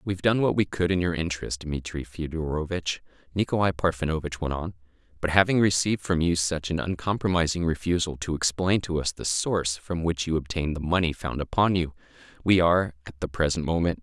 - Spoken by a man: Yes, male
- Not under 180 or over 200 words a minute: Yes, average, 190 wpm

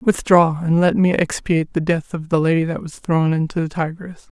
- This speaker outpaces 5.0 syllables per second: Yes, 5.2 syllables/s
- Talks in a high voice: No, medium, 165 Hz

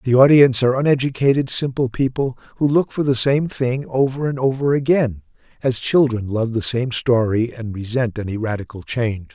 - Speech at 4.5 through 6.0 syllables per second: Yes, 5.3 syllables/s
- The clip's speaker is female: No, male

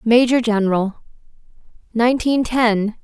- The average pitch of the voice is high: Yes, high, 230 Hz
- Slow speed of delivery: Yes, slow, 80 wpm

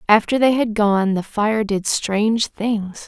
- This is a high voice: Yes, high, 215 Hz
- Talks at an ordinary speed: Yes, average, 175 wpm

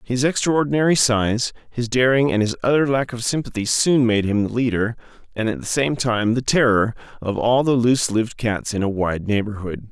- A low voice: Yes, low, 120 Hz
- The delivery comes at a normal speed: Yes, average, 190 wpm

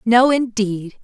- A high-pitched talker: Yes, high, 225 Hz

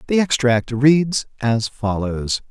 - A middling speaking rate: No, slow, 120 wpm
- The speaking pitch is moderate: No, low, 130 Hz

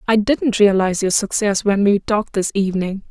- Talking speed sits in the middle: Yes, average, 195 wpm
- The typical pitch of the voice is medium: No, high, 205 Hz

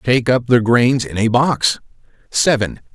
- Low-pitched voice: Yes, low, 120 Hz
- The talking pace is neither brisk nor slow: Yes, average, 165 wpm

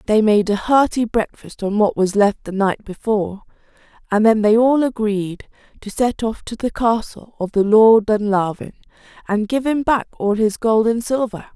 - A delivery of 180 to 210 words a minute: Yes, average, 190 wpm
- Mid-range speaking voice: No, high, 220 Hz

